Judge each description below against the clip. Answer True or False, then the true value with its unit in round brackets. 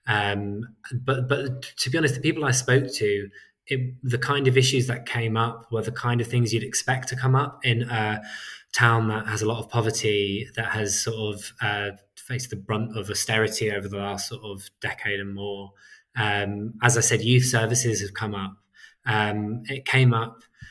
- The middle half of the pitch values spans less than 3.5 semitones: True (3.1 semitones)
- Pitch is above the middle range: False (115 Hz)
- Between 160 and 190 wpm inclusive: False (200 wpm)